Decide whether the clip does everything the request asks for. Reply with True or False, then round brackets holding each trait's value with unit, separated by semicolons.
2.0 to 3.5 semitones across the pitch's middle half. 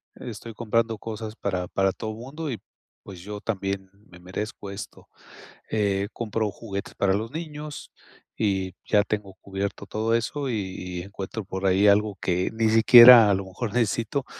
True (2.8 semitones)